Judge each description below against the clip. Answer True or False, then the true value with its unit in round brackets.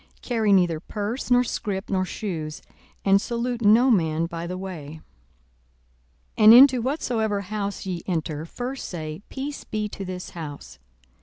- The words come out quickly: False (155 wpm)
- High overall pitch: True (200 Hz)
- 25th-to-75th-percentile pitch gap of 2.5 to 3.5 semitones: False (5.6 semitones)